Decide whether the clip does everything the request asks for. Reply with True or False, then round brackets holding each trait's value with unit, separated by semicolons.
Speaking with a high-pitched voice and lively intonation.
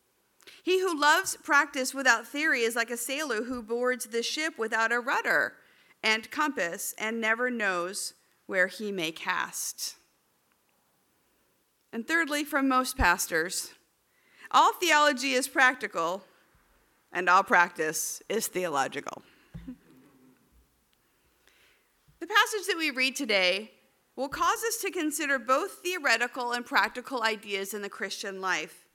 True (250 Hz; 6.5 semitones)